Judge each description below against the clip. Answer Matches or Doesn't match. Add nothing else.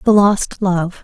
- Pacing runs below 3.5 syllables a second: Matches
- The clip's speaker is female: Matches